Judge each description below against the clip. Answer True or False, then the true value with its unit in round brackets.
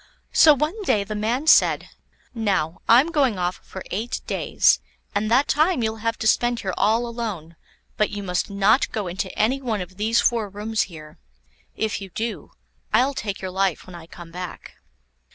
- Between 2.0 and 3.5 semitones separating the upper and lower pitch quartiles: False (3.9 semitones)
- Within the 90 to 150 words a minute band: False (185 wpm)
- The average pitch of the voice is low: False (215 Hz)